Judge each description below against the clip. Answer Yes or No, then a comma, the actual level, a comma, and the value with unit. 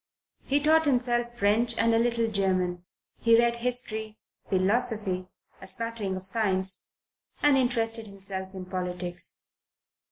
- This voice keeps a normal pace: No, slow, 125 wpm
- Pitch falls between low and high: No, high, 220 Hz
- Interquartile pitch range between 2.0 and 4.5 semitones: Yes, average, 4.0 semitones